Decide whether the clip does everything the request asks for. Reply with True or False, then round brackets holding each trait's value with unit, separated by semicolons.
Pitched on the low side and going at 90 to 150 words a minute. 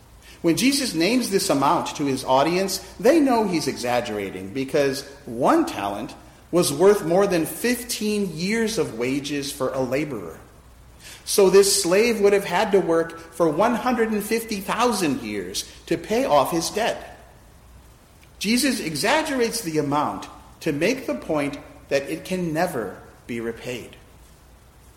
False (175 Hz; 135 wpm)